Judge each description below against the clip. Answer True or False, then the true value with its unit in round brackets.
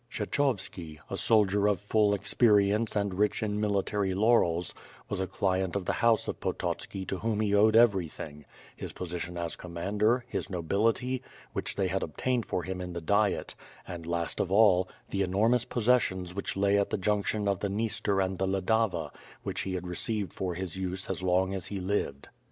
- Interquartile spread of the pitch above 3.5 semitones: False (2.5 semitones)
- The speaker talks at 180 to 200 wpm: True (190 wpm)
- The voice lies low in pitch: True (100 Hz)